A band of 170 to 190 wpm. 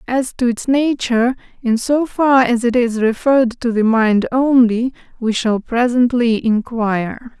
No: average, 155 wpm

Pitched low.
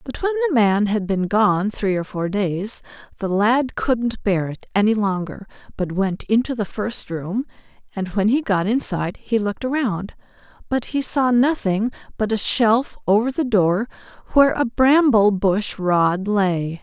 No: high, 215 Hz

